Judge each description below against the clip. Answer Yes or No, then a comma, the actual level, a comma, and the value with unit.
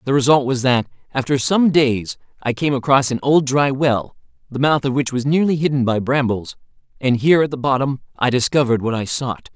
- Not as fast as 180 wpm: No, fast, 205 wpm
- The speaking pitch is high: No, low, 130 Hz